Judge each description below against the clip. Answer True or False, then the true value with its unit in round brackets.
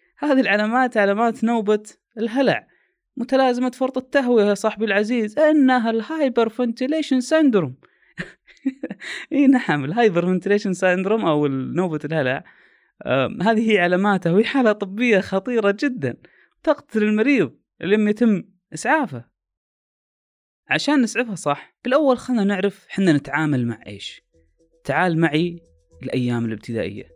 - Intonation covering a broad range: True (7.4 semitones)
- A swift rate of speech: False (115 wpm)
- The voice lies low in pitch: False (210 Hz)